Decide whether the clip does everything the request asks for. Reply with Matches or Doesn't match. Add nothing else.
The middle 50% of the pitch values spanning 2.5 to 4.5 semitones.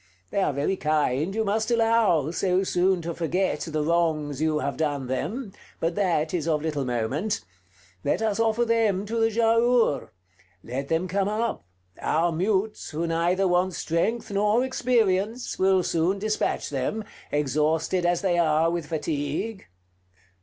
Doesn't match